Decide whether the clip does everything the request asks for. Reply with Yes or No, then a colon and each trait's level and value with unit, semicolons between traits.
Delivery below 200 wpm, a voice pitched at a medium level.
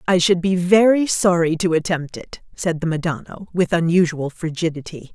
Yes: average, 165 wpm; medium, 170 Hz